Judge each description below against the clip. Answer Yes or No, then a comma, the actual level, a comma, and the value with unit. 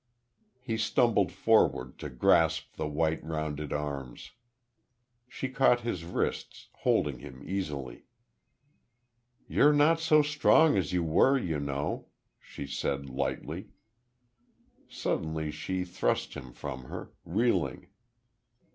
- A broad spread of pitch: Yes, wide, 8.4 semitones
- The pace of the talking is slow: Yes, slow, 110 wpm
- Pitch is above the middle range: No, very low, 80 Hz